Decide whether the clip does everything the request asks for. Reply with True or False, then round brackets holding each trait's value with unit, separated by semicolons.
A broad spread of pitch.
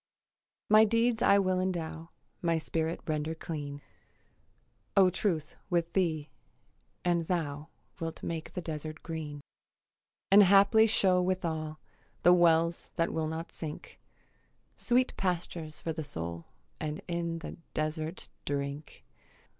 False (2.7 semitones)